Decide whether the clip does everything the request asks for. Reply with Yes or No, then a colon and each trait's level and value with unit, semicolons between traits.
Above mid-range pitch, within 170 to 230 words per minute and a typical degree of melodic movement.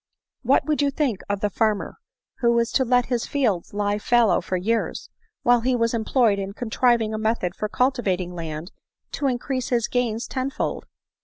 Yes: high, 230 Hz; average, 180 wpm; average, 3.4 semitones